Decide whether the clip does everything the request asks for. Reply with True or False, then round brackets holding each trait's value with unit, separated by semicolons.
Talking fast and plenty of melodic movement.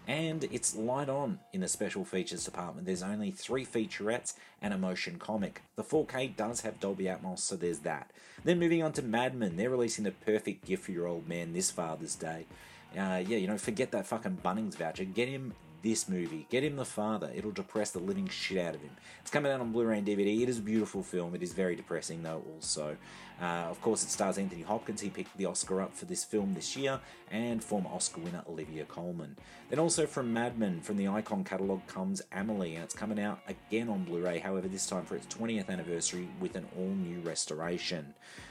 True (220 wpm; 6.3 semitones)